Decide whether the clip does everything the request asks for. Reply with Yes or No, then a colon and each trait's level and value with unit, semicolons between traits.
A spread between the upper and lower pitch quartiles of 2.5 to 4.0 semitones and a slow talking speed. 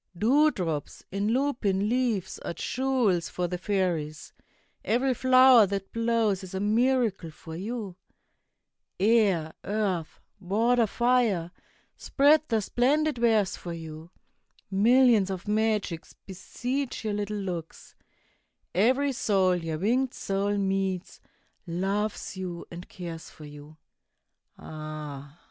No: average, 5.2 semitones; slow, 115 wpm